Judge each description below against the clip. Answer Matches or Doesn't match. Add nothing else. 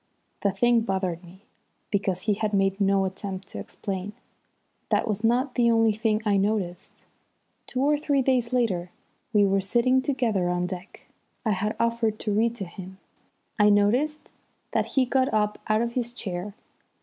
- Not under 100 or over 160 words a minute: Doesn't match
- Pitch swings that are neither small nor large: Matches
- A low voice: Doesn't match